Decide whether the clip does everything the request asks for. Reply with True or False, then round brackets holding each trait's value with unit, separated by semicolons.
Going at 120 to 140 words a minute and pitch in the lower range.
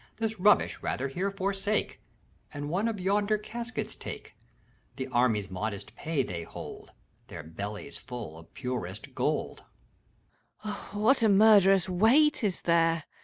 False (135 wpm; 180 Hz)